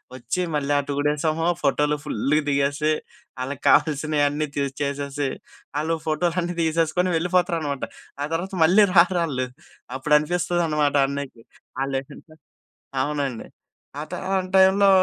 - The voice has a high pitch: No, medium, 150 Hz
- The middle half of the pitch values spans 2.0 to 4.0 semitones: Yes, average, 3.0 semitones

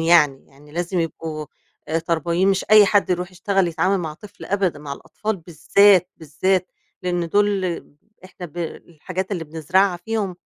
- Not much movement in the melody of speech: No, average, 3.0 semitones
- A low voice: No, medium, 175 Hz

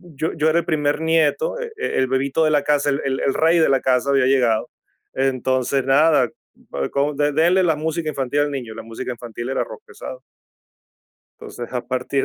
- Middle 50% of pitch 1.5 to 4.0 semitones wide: Yes, average, 3.5 semitones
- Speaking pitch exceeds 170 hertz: No, medium, 140 Hz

